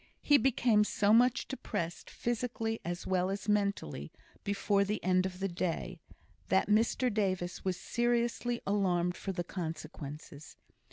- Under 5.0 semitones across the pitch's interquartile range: Yes, average, 4.1 semitones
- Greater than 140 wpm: No, slow, 135 wpm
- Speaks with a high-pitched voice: Yes, high, 195 Hz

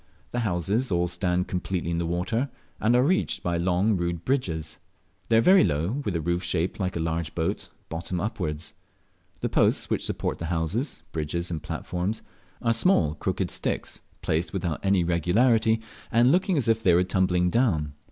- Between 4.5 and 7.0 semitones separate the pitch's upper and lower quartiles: Yes, average, 5.0 semitones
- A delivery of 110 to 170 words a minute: No, average, 180 wpm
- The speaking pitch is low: Yes, very low, 90 Hz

